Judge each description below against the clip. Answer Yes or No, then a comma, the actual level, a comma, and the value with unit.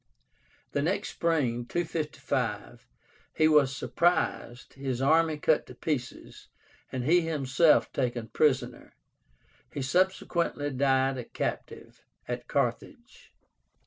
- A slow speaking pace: Yes, slow, 105 wpm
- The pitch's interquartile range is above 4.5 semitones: No, average, 4.0 semitones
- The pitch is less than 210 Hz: Yes, low, 135 Hz